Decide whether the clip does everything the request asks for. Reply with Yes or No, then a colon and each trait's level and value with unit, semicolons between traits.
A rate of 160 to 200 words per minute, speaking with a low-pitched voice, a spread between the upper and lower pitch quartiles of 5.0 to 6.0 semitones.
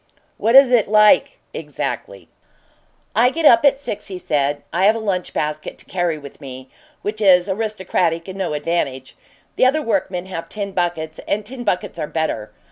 No: average, 180 wpm; medium, 185 Hz; wide, 5.4 semitones